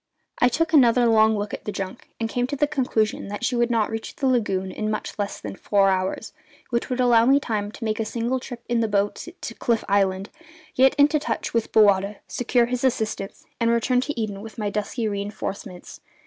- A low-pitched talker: No, high, 225 Hz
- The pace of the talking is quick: Yes, fast, 215 wpm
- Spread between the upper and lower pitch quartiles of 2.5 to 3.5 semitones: Yes, average, 3.2 semitones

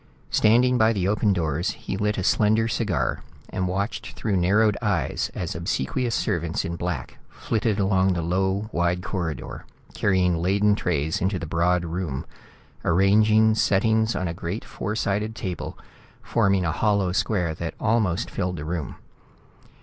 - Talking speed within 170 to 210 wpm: No, average, 150 wpm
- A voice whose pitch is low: Yes, very low, 95 Hz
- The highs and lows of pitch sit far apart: No, average, 3.7 semitones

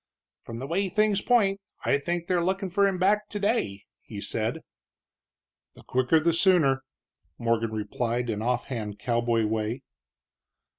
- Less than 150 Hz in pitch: Yes, medium, 140 Hz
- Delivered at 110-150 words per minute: Yes, average, 140 wpm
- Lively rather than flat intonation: Yes, wide, 8.5 semitones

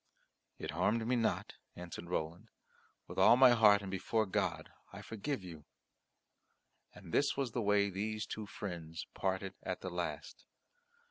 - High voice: No, low, 100 Hz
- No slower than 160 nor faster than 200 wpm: No, average, 150 wpm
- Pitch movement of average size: Yes, average, 3.9 semitones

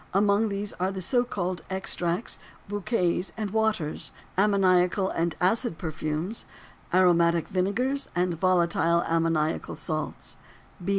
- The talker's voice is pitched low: No, medium, 185 Hz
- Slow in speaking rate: Yes, slow, 110 wpm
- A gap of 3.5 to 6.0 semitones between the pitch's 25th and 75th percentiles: No, average, 3.1 semitones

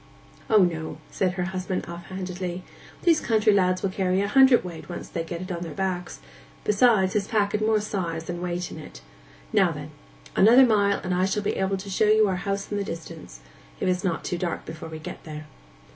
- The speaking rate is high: Yes, fast, 215 wpm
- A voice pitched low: No, medium, 185 Hz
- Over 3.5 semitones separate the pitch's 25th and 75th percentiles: No, average, 2.8 semitones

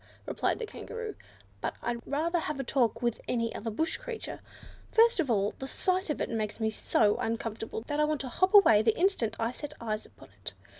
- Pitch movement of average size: No, wide, 7.1 semitones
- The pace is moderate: No, fast, 210 wpm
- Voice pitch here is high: Yes, very high, 250 Hz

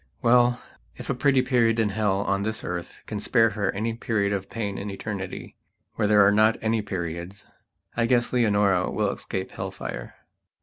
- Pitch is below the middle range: Yes, low, 105 Hz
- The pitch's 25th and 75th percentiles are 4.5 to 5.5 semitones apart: No, narrow, 2.6 semitones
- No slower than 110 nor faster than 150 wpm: No, average, 170 wpm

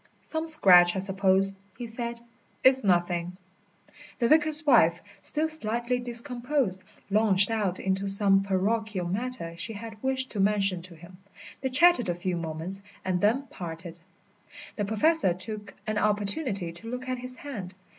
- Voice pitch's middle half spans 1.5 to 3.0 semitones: No, average, 5.0 semitones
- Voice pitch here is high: Yes, high, 205 Hz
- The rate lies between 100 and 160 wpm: Yes, average, 150 wpm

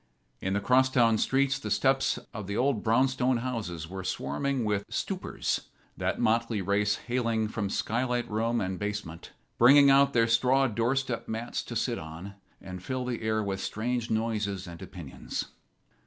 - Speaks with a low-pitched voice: Yes, low, 115 Hz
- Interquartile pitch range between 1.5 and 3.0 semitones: No, average, 4.0 semitones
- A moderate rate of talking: Yes, average, 165 wpm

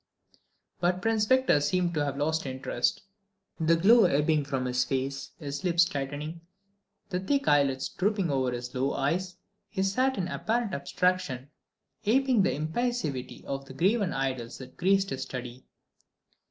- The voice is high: No, medium, 155 Hz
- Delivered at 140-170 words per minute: Yes, average, 150 wpm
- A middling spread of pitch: No, wide, 6.0 semitones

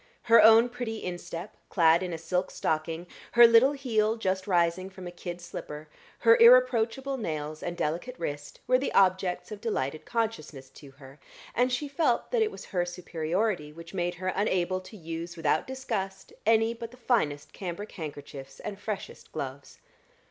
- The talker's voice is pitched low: No, medium, 185 Hz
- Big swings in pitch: Yes, wide, 5.7 semitones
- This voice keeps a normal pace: Yes, average, 170 wpm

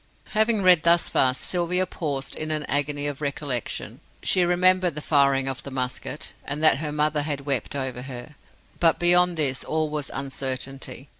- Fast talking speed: No, average, 170 wpm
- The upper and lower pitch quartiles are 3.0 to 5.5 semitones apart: Yes, average, 3.8 semitones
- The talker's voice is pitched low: No, medium, 150 Hz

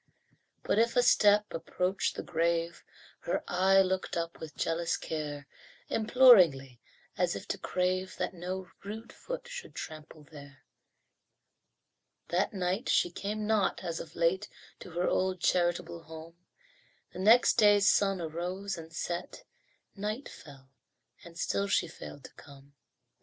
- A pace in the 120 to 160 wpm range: Yes, average, 140 wpm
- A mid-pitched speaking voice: Yes, medium, 180 Hz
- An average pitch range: Yes, average, 3.5 semitones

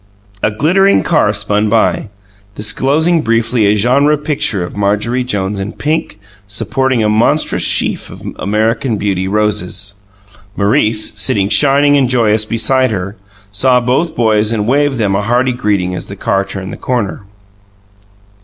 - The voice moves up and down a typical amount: Yes, average, 4.1 semitones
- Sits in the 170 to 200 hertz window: No, low, 110 Hz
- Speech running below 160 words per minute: Yes, average, 145 wpm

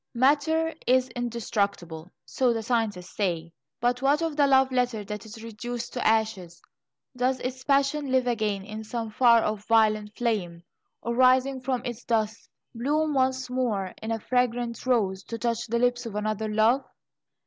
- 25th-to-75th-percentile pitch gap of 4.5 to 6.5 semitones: No, average, 3.1 semitones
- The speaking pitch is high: Yes, high, 235 Hz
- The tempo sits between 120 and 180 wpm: Yes, average, 165 wpm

